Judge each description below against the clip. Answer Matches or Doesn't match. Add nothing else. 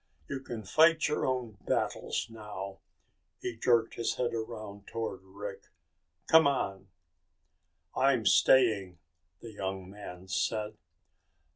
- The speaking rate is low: Matches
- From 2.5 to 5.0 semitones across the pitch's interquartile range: Matches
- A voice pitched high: Doesn't match